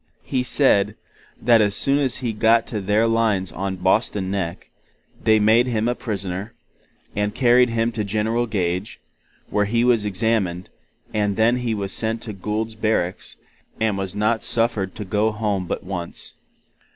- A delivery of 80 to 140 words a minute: No, average, 165 wpm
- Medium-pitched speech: No, low, 110 Hz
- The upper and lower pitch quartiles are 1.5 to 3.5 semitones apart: Yes, narrow, 2.6 semitones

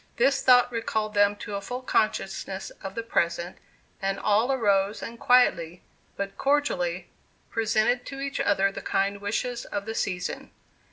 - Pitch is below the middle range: No, high, 215 Hz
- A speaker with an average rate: Yes, average, 155 wpm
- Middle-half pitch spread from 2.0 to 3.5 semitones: No, average, 3.9 semitones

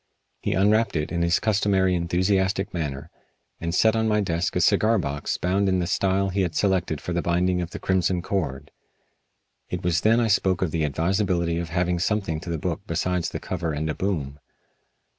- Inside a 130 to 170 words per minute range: No, average, 200 wpm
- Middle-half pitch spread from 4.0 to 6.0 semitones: No, narrow, 2.5 semitones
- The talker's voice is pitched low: Yes, very low, 90 Hz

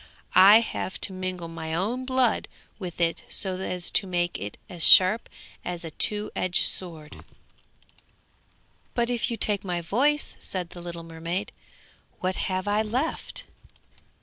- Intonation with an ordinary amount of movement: Yes, average, 3.6 semitones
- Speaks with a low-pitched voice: No, medium, 185 Hz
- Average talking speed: Yes, average, 150 wpm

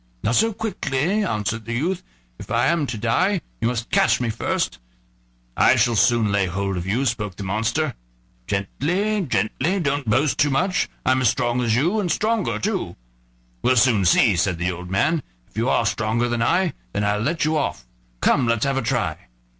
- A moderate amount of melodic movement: No, wide, 6.7 semitones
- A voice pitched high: No, low, 120 Hz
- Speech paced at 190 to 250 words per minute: Yes, average, 195 wpm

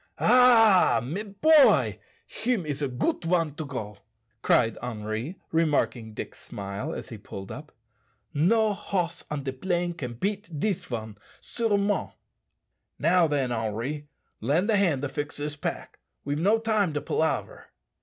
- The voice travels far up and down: Yes, wide, 7.7 semitones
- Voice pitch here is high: No, medium, 155 Hz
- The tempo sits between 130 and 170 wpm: Yes, average, 145 wpm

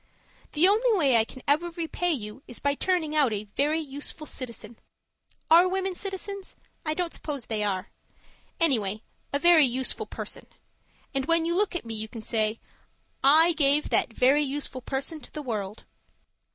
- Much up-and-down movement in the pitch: Yes, wide, 6.0 semitones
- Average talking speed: Yes, average, 170 wpm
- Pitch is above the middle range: Yes, very high, 290 Hz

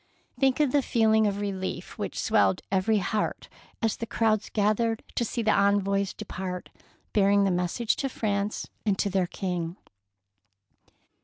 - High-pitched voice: Yes, high, 205 Hz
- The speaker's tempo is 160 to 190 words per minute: No, average, 150 wpm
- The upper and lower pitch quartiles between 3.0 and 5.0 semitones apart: No, narrow, 2.5 semitones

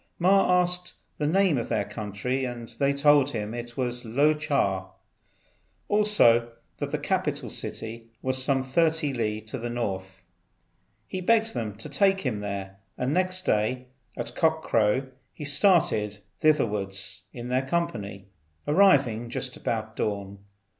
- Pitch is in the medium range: No, low, 125 Hz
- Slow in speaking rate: No, average, 145 wpm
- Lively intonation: Yes, wide, 6.1 semitones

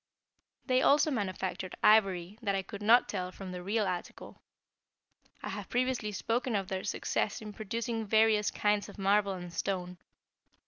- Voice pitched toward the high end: Yes, high, 205 Hz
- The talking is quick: No, average, 155 wpm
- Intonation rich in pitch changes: No, average, 2.9 semitones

